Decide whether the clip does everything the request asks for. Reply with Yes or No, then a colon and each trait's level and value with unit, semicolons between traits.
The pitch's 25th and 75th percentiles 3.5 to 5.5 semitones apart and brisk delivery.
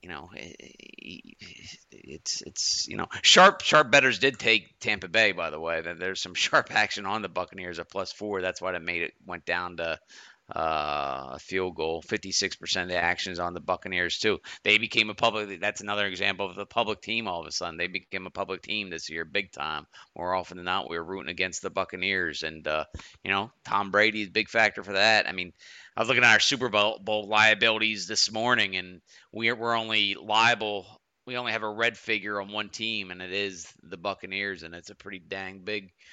No: average, 3.0 semitones; fast, 215 wpm